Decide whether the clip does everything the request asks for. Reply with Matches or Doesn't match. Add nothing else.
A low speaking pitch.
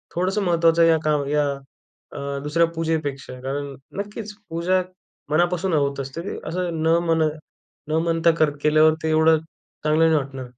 Doesn't match